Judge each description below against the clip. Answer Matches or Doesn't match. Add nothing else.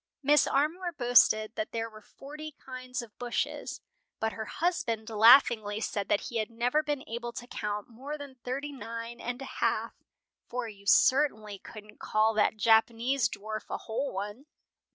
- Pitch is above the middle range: Matches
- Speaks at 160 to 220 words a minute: Matches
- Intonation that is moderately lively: Matches